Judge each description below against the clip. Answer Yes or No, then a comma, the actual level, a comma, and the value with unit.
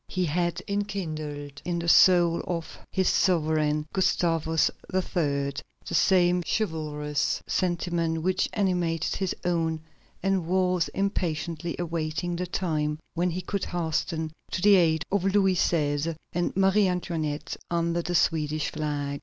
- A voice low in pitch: No, medium, 170 Hz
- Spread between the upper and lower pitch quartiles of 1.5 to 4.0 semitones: Yes, average, 2.7 semitones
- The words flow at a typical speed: No, slow, 130 wpm